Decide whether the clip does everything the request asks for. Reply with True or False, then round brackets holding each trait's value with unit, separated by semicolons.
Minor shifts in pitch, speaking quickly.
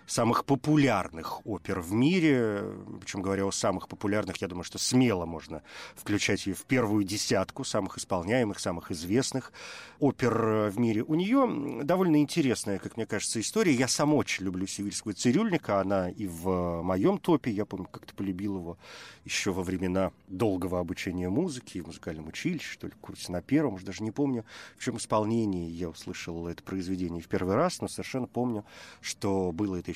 False (4.8 semitones; 170 wpm)